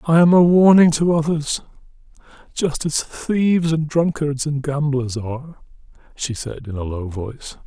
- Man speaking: Yes, male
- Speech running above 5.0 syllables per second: No, 4.5 syllables/s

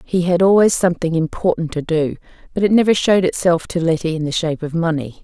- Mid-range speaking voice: Yes, medium, 170 Hz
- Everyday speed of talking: No, fast, 220 wpm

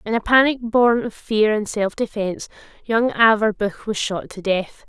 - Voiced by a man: No, female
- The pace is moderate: Yes, average, 185 wpm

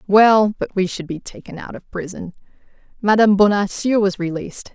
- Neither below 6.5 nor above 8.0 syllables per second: No, 5.5 syllables/s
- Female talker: Yes, female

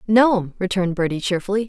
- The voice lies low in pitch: No, high, 195 Hz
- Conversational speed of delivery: Yes, average, 145 wpm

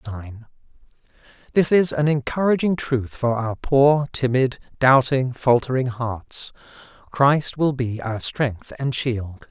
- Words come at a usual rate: No, slow, 125 wpm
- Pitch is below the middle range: Yes, low, 130 Hz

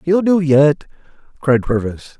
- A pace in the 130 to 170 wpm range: Yes, slow, 135 wpm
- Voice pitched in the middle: Yes, medium, 145 Hz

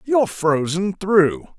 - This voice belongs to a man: Yes, male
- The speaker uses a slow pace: Yes, slow, 115 wpm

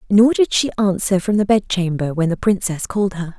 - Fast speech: Yes, fast, 215 wpm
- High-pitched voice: Yes, high, 195 Hz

